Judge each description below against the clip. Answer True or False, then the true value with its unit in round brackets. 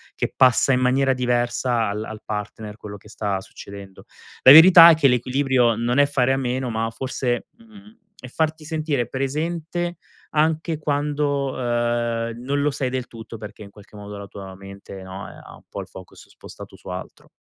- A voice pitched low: True (125 Hz)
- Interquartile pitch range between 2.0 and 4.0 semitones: False (4.7 semitones)